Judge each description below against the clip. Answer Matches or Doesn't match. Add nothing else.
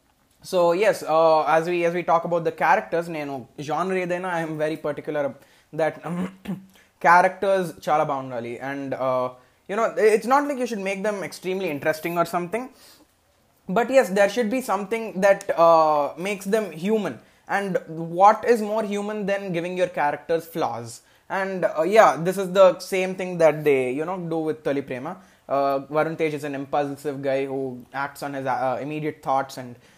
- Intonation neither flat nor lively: Matches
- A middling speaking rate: Doesn't match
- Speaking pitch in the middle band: Matches